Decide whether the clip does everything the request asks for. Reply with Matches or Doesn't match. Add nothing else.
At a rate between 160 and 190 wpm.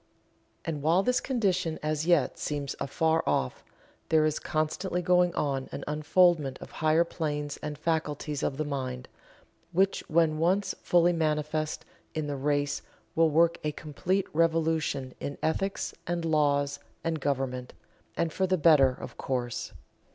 Doesn't match